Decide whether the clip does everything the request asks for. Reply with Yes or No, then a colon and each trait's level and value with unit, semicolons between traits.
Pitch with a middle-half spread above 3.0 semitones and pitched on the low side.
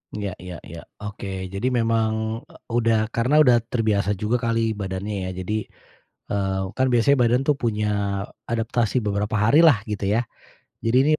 No: average, 2.7 semitones; low, 110 Hz